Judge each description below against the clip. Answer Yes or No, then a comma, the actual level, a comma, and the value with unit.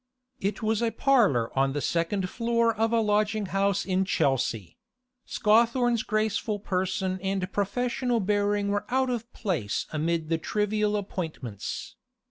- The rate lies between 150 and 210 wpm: No, slow, 135 wpm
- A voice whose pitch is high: Yes, high, 205 Hz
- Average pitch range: Yes, average, 3.5 semitones